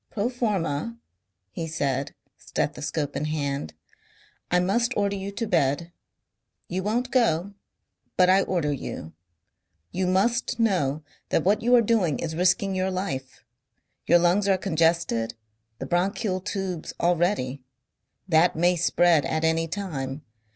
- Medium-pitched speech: Yes, medium, 175 Hz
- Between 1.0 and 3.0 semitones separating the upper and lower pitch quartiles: No, average, 4.2 semitones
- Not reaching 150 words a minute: Yes, slow, 135 wpm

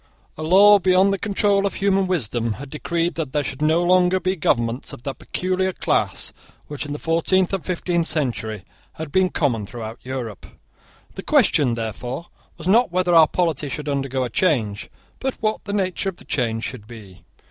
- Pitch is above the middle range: No, medium, 160 Hz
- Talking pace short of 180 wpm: No, average, 185 wpm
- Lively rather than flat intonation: Yes, wide, 6.8 semitones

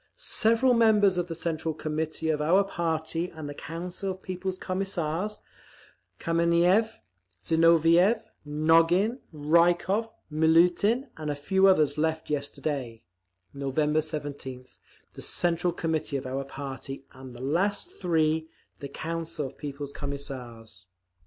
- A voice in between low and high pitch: Yes, medium, 160 Hz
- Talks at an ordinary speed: No, slow, 120 wpm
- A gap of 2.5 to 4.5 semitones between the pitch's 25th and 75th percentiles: Yes, average, 3.7 semitones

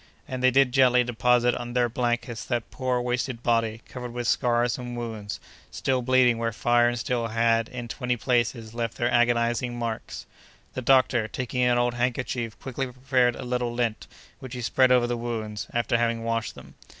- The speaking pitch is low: Yes, low, 120 Hz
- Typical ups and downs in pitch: No, narrow, 1.2 semitones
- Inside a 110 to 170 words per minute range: No, average, 185 wpm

